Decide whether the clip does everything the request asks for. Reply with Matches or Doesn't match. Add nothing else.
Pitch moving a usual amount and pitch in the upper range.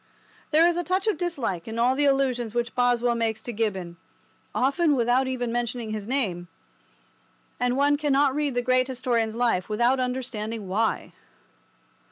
Matches